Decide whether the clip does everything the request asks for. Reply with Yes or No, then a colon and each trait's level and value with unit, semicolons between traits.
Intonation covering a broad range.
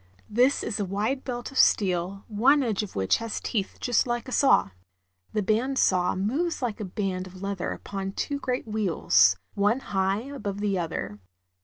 No: average, 4.3 semitones